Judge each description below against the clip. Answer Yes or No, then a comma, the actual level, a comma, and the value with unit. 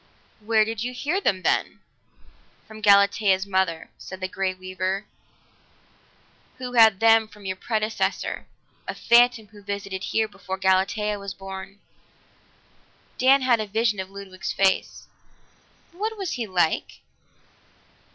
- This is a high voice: Yes, high, 205 Hz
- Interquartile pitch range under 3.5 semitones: Yes, average, 2.9 semitones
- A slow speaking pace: Yes, slow, 130 wpm